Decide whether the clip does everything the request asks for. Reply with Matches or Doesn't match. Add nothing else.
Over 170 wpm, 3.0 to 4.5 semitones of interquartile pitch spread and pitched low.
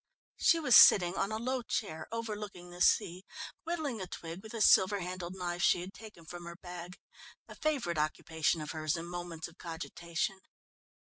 Doesn't match